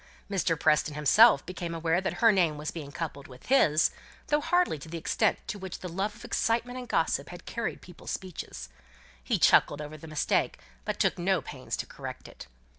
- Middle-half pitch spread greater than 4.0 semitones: Yes, average, 4.7 semitones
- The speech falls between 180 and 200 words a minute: Yes, average, 195 wpm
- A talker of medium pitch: Yes, medium, 170 Hz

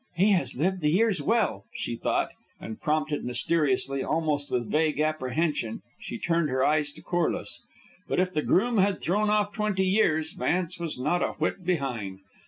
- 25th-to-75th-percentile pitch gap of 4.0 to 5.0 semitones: Yes, average, 4.7 semitones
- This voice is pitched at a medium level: Yes, medium, 160 Hz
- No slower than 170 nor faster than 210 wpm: Yes, average, 175 wpm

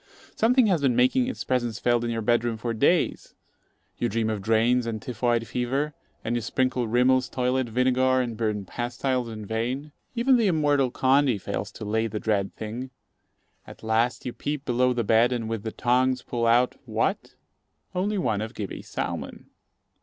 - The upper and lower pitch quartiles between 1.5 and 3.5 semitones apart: Yes, narrow, 2.5 semitones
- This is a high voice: No, low, 120 Hz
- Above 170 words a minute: Yes, average, 180 wpm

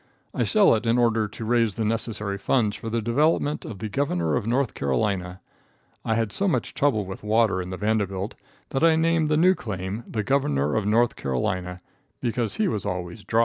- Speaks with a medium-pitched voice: No, low, 110 Hz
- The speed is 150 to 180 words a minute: No, average, 200 wpm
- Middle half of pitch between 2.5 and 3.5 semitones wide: No, average, 4.1 semitones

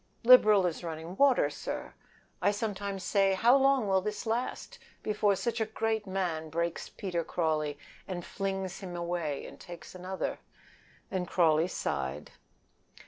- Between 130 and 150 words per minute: Yes, average, 140 wpm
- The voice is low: No, high, 190 Hz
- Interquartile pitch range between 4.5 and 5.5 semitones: No, average, 3.7 semitones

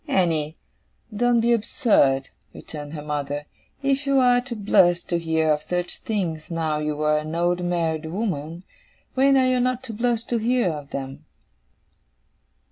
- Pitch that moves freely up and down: Yes, wide, 7.7 semitones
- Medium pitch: Yes, medium, 175 Hz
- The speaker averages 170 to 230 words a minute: No, average, 160 wpm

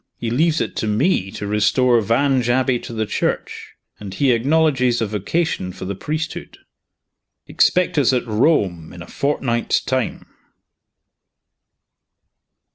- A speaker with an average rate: No, slow, 130 wpm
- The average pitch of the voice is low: Yes, low, 120 Hz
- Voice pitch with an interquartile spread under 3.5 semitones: No, average, 5.1 semitones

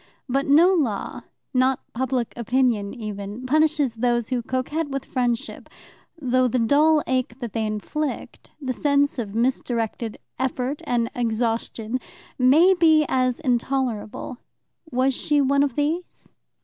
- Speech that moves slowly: Yes, slow, 130 wpm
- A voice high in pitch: Yes, very high, 255 Hz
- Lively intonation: No, average, 3.2 semitones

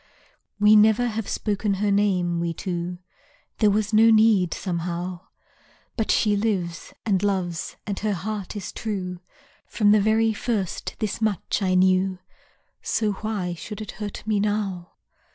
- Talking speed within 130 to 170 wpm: Yes, average, 150 wpm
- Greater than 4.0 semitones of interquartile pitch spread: No, average, 2.8 semitones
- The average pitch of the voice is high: Yes, high, 205 Hz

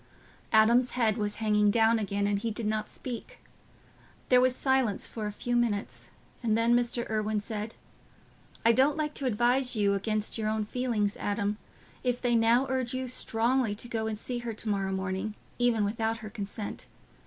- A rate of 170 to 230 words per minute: Yes, average, 185 wpm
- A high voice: Yes, high, 225 Hz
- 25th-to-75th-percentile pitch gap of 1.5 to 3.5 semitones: Yes, narrow, 2.6 semitones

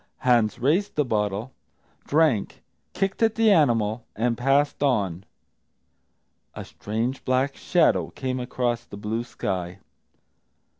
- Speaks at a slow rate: Yes, slow, 115 wpm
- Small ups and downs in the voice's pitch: No, average, 4.9 semitones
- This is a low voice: Yes, low, 125 Hz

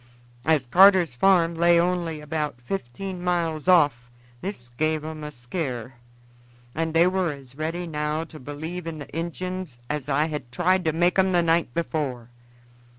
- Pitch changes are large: No, average, 3.3 semitones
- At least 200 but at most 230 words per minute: No, average, 160 wpm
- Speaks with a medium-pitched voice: Yes, medium, 160 Hz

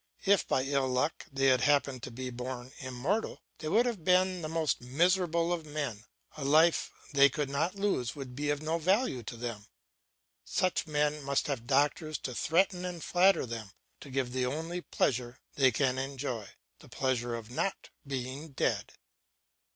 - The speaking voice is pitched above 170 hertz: No, medium, 140 Hz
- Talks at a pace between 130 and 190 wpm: Yes, average, 175 wpm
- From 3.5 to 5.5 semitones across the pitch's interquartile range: Yes, average, 4.4 semitones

